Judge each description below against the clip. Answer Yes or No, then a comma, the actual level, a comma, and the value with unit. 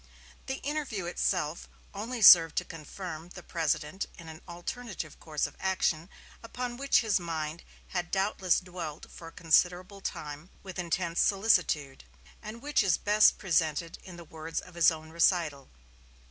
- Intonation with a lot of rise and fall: No, average, 3.5 semitones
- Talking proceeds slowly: No, average, 150 wpm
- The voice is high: No, medium, 175 Hz